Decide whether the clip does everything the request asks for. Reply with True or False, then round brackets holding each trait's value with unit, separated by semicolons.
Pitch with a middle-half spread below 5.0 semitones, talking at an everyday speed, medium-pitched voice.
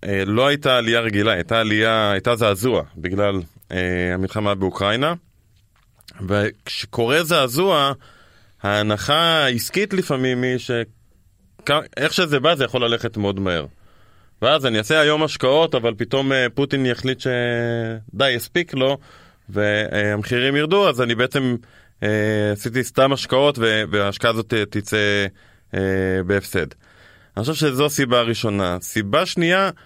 False (4.4 semitones; 120 wpm; 115 Hz)